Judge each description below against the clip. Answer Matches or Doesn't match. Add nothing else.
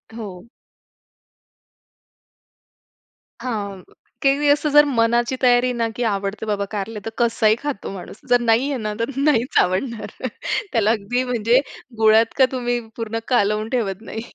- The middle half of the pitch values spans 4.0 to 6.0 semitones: Doesn't match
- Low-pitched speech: Doesn't match